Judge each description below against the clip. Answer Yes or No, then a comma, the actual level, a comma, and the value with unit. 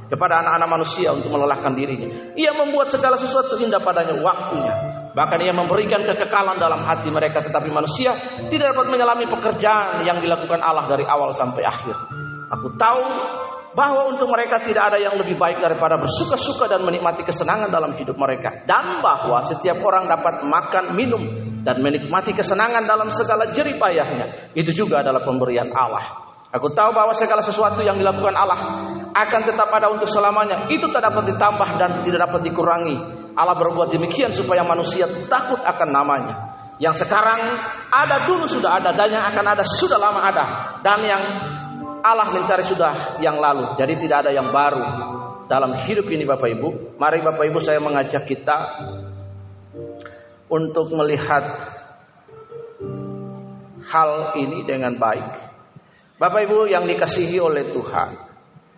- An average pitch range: No, wide, 6.3 semitones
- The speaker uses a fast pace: Yes, fast, 150 wpm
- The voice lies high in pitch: No, medium, 170 Hz